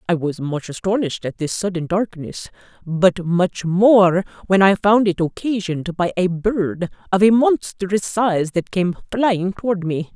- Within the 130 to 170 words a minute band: Yes, average, 165 wpm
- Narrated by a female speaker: Yes, female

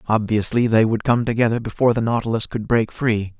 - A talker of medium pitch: No, low, 115 Hz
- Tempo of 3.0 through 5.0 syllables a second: No, 6.0 syllables/s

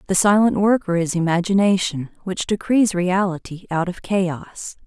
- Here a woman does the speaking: Yes, female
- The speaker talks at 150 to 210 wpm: No, slow, 135 wpm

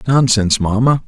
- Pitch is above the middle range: No, low, 115 Hz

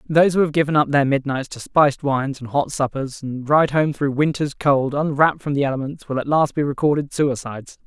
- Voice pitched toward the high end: No, medium, 140 Hz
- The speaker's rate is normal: No, fast, 220 wpm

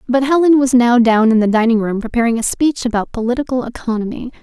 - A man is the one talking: No, female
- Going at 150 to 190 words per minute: No, fast, 205 wpm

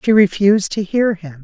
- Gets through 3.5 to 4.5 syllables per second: No, 5.3 syllables/s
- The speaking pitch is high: Yes, high, 195 Hz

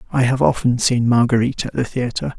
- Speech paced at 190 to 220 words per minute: Yes, average, 200 wpm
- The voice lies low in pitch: Yes, low, 120 Hz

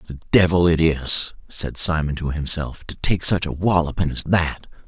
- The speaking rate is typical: Yes, average, 195 wpm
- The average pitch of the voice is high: No, very low, 85 Hz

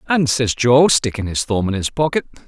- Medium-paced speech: No, fast, 220 wpm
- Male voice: Yes, male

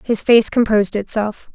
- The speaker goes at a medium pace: Yes, average, 155 wpm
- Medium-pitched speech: No, high, 220 Hz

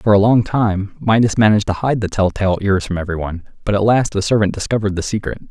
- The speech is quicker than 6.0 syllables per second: Yes, 6.5 syllables/s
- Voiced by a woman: No, male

